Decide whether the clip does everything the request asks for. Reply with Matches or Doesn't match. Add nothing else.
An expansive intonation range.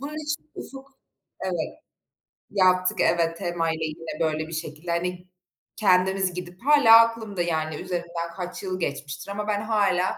Doesn't match